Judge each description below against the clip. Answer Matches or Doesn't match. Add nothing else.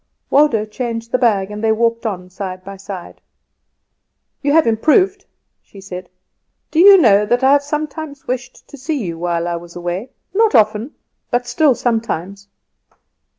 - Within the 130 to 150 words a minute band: Doesn't match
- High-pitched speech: Matches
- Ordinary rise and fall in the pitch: Doesn't match